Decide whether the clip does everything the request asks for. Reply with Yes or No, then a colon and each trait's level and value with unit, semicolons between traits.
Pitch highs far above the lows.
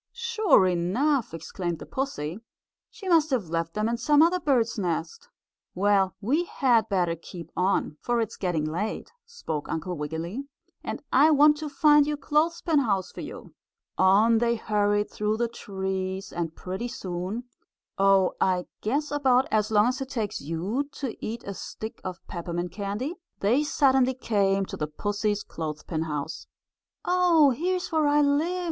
Yes: wide, 7.4 semitones